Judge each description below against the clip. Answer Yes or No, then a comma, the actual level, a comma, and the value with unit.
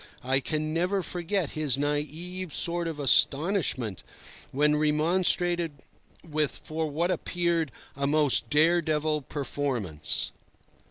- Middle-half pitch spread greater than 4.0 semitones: No, average, 3.0 semitones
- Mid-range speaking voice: Yes, medium, 155 Hz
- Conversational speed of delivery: No, slow, 110 wpm